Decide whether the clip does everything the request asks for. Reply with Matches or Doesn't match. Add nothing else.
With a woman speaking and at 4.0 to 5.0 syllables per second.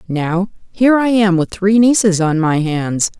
Matches